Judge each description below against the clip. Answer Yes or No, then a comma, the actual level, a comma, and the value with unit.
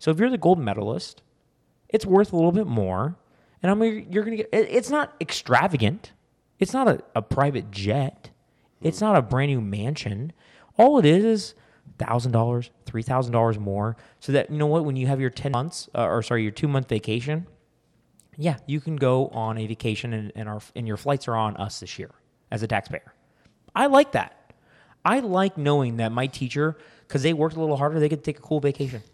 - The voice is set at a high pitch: No, medium, 140 Hz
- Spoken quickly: Yes, fast, 210 wpm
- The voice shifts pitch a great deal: Yes, wide, 6.1 semitones